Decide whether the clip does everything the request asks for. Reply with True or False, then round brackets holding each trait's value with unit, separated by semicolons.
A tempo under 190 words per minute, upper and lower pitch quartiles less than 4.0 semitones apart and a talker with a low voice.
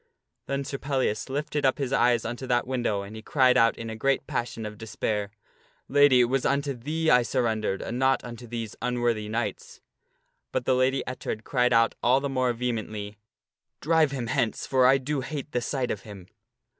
False (195 wpm; 2.9 semitones; 125 Hz)